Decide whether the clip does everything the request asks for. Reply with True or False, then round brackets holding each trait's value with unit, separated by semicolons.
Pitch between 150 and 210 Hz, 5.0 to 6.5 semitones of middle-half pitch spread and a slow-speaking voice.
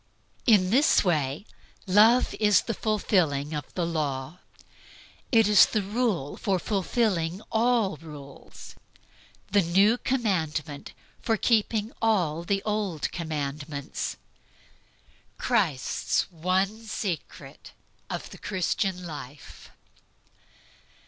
True (185 Hz; 5.6 semitones; 95 wpm)